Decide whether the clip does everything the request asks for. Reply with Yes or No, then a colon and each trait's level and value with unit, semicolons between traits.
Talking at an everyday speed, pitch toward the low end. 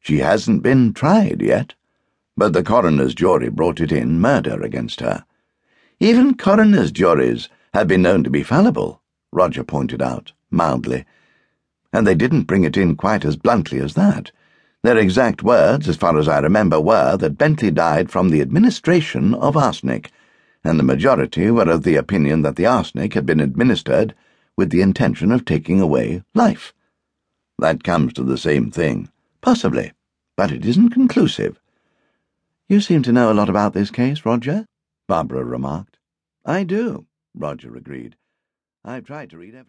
Yes: average, 165 wpm; low, 130 Hz